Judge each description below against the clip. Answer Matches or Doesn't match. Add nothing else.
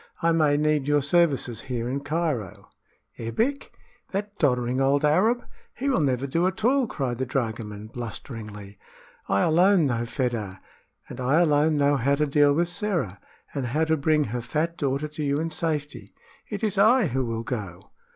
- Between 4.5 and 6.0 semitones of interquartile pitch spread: Matches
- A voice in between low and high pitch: Matches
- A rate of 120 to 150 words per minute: Doesn't match